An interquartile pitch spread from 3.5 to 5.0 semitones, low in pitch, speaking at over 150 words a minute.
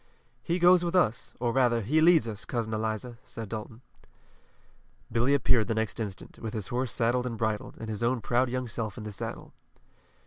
No: narrow, 2.5 semitones; low, 115 Hz; average, 195 wpm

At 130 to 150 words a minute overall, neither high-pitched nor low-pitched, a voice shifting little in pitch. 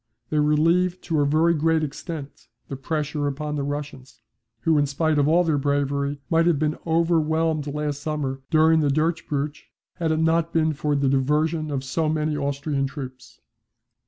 No: average, 170 wpm; medium, 150 Hz; narrow, 2.1 semitones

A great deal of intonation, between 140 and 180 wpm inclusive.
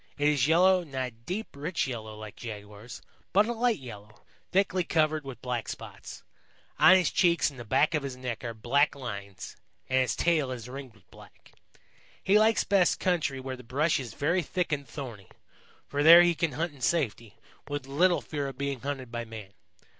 No: wide, 5.9 semitones; average, 195 wpm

